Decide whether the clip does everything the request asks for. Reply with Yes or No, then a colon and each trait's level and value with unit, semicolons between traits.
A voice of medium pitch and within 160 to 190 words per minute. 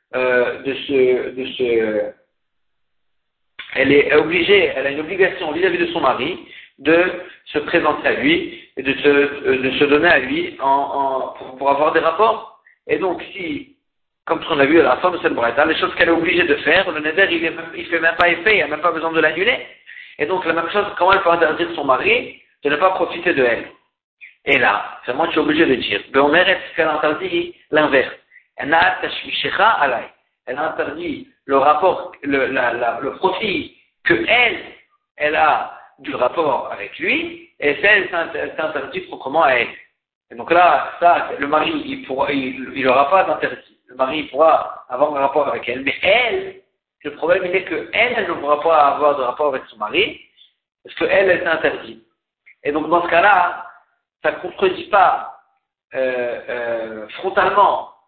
Yes: medium, 170 Hz; average, 185 wpm